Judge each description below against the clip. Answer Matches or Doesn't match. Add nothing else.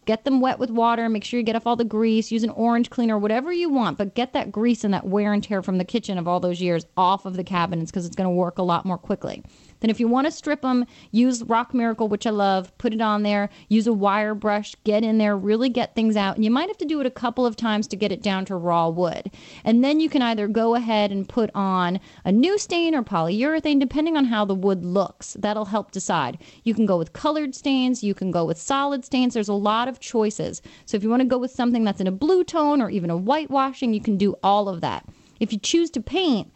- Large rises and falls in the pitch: Doesn't match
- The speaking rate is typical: Doesn't match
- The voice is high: Matches